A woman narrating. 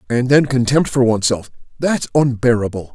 No: male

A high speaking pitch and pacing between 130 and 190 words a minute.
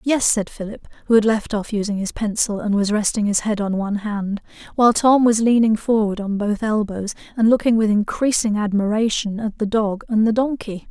No: high, 215 Hz; fast, 205 wpm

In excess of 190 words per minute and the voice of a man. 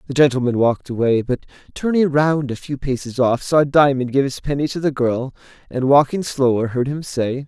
Yes: average, 200 wpm; male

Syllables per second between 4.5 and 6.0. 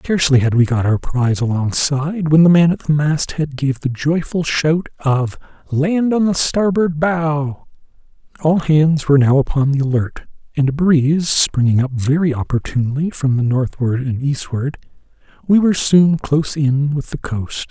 Yes: 4.7 syllables/s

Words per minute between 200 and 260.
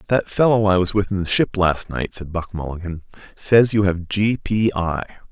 No: average, 190 wpm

